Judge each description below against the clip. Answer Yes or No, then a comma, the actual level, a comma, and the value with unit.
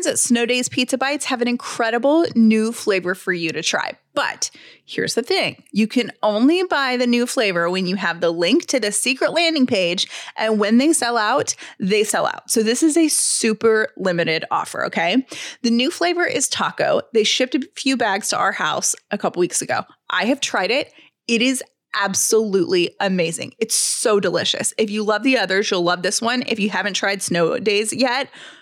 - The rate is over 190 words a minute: Yes, average, 200 wpm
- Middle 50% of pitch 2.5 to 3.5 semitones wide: No, average, 4.9 semitones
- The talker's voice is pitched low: No, high, 230 Hz